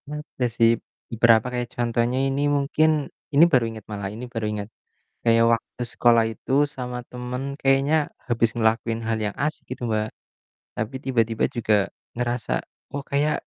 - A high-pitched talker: No, low, 120 Hz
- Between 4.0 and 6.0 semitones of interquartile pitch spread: No, average, 2.8 semitones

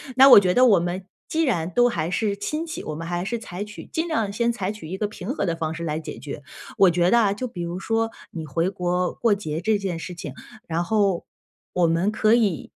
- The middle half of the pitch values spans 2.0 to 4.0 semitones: No, average, 4.5 semitones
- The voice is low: No, high, 190 Hz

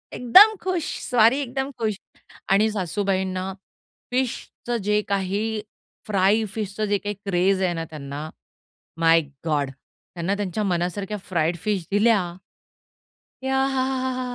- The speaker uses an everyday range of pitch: Yes, average, 4.6 semitones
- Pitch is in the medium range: No, high, 205 Hz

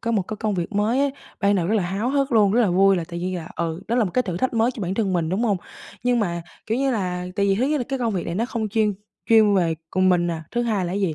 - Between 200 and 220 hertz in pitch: Yes, high, 205 Hz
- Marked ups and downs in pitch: No, average, 4.4 semitones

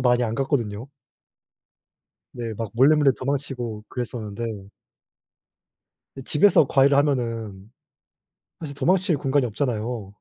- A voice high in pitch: No, low, 125 Hz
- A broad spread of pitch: No, average, 4.0 semitones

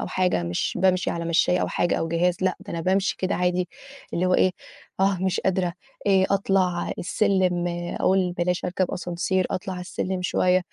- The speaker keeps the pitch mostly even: Yes, narrow, 1.3 semitones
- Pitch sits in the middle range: Yes, medium, 180 Hz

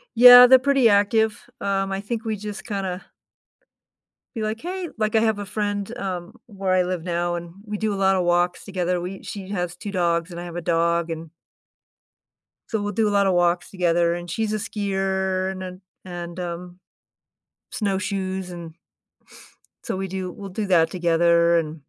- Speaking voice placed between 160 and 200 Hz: Yes, high, 190 Hz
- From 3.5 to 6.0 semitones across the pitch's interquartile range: No, average, 2.9 semitones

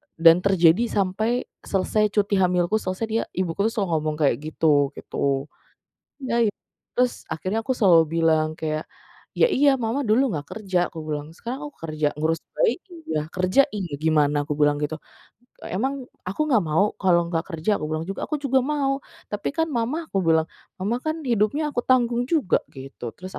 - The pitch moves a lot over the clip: Yes, wide, 7.5 semitones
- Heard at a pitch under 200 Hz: Yes, high, 190 Hz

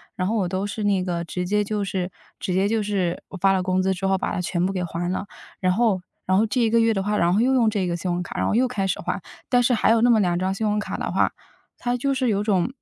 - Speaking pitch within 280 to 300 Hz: No, high, 195 Hz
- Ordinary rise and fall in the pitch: Yes, average, 3.3 semitones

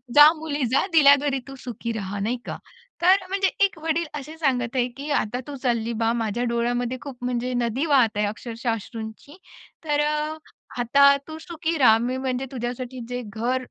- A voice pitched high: Yes, very high, 255 Hz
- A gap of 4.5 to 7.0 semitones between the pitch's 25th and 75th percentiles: No, average, 3.8 semitones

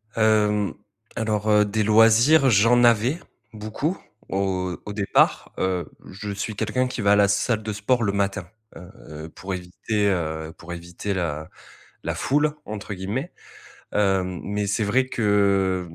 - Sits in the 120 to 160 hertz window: No, low, 105 Hz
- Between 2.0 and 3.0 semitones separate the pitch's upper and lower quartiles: Yes, narrow, 2.6 semitones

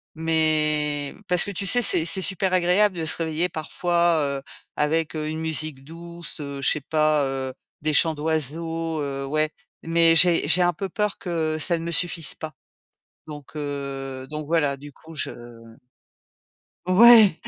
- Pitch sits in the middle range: Yes, medium, 160 Hz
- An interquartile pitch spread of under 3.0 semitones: Yes, narrow, 2.6 semitones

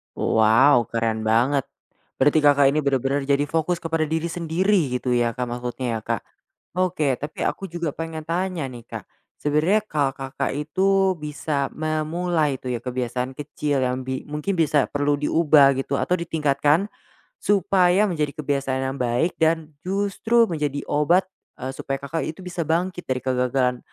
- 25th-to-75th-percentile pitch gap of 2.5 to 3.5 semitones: No, average, 4.0 semitones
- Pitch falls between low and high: Yes, medium, 145 Hz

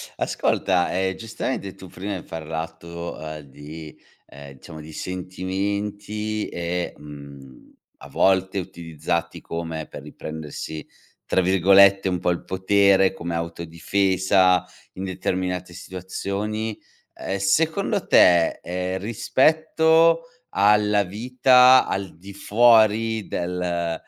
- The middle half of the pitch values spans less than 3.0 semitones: No, average, 3.3 semitones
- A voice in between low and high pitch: No, very low, 95 Hz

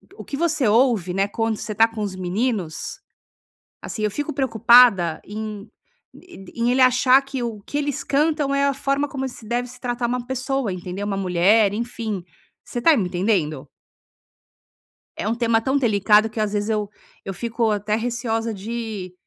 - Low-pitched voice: No, high, 225 Hz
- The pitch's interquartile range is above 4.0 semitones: No, average, 3.6 semitones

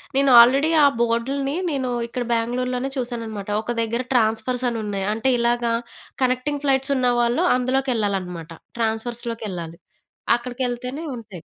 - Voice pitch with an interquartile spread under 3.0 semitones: Yes, narrow, 2.4 semitones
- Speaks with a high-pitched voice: Yes, high, 240 Hz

